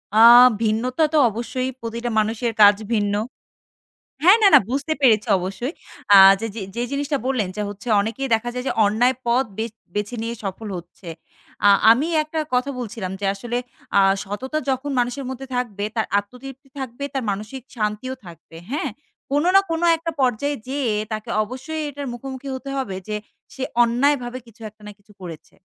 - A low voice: No, high, 240 Hz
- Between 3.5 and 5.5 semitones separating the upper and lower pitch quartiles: Yes, average, 4.1 semitones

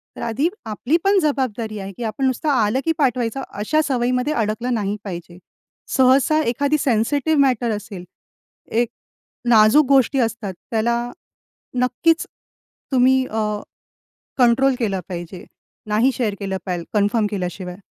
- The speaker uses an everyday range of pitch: Yes, average, 4.0 semitones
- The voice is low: No, high, 235 Hz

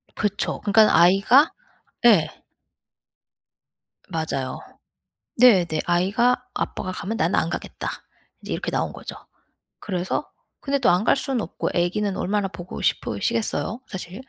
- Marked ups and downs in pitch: No, average, 4.4 semitones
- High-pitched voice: Yes, high, 195 Hz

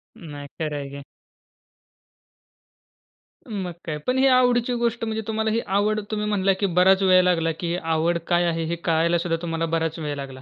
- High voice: No, medium, 175 Hz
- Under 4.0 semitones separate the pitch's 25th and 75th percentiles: No, average, 4.5 semitones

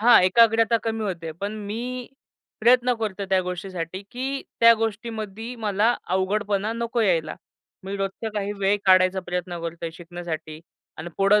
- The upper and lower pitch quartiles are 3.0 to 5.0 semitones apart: Yes, average, 3.7 semitones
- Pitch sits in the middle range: No, high, 200 Hz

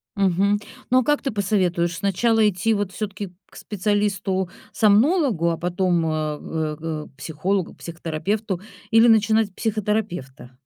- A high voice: Yes, high, 195 Hz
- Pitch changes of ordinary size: Yes, average, 4.0 semitones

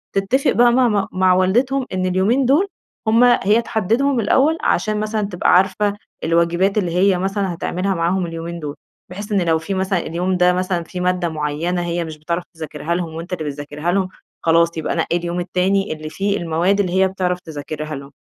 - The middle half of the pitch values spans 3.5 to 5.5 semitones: No, average, 3.0 semitones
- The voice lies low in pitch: No, medium, 180 Hz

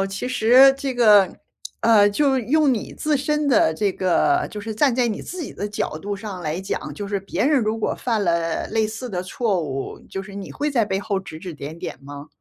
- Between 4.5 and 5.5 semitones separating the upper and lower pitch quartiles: Yes, average, 4.9 semitones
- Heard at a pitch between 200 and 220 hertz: Yes, high, 210 Hz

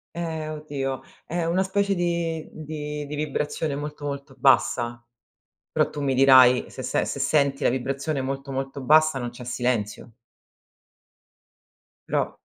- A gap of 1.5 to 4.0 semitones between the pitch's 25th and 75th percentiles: Yes, average, 2.8 semitones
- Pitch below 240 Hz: Yes, medium, 140 Hz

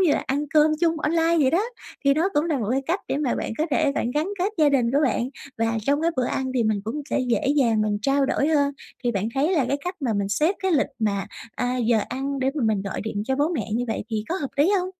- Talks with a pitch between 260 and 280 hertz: Yes, very high, 275 Hz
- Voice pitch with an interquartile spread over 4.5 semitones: Yes, average, 4.9 semitones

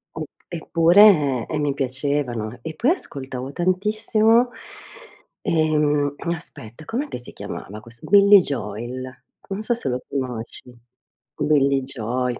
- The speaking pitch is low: No, medium, 145 Hz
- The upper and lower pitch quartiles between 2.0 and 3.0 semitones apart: No, wide, 5.7 semitones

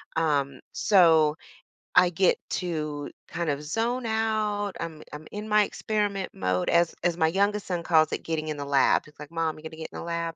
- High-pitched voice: No, medium, 165 Hz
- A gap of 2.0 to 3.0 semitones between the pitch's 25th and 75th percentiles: No, average, 4.6 semitones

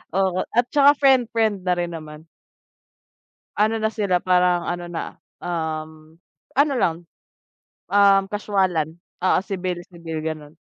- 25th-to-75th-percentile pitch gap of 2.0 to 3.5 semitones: No, average, 4.2 semitones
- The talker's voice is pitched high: No, medium, 180 Hz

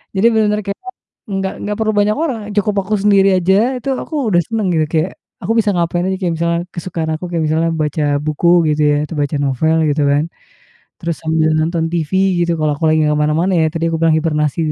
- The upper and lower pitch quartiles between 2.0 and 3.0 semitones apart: No, average, 3.5 semitones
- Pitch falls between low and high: Yes, medium, 165 Hz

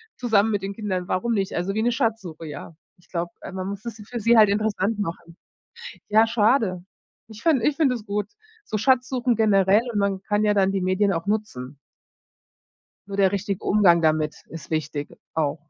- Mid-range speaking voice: No, high, 200 Hz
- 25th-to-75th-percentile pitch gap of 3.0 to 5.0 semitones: Yes, average, 3.4 semitones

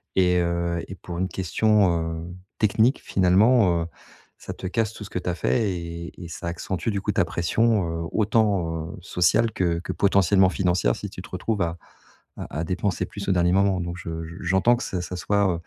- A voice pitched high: No, very low, 90 Hz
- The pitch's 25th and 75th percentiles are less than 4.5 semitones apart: Yes, average, 2.8 semitones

